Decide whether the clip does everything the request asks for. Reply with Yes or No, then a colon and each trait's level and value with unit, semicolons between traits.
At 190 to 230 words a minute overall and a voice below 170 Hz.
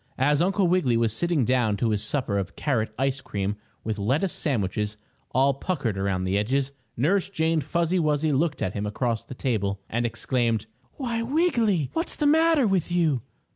No: average, 175 wpm; low, 135 Hz